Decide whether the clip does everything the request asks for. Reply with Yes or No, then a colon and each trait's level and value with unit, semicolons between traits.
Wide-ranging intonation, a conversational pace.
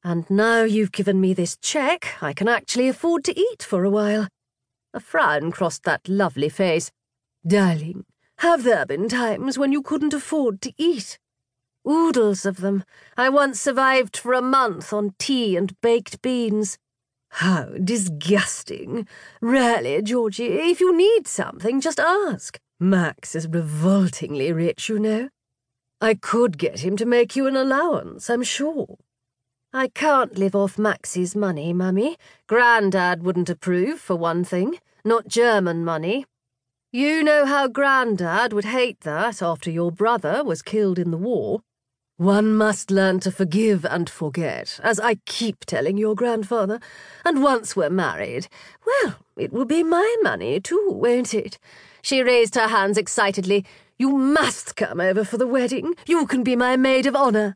Yes: wide, 6.2 semitones; average, 155 wpm